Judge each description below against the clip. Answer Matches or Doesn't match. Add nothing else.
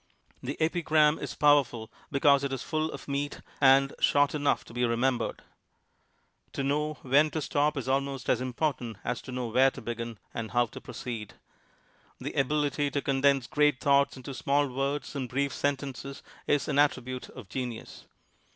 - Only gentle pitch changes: Matches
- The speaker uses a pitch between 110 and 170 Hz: Matches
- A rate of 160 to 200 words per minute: Matches